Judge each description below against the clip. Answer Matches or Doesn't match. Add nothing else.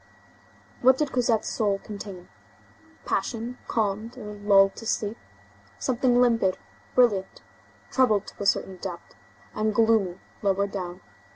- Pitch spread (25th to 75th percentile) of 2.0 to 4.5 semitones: Matches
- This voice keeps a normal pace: Doesn't match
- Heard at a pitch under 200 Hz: Doesn't match